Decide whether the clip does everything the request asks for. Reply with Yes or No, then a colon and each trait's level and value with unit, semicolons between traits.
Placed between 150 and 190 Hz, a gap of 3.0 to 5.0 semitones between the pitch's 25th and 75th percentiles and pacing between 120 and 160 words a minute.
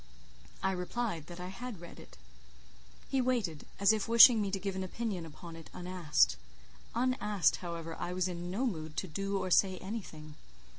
No: medium, 185 Hz; average, 3.7 semitones; average, 180 wpm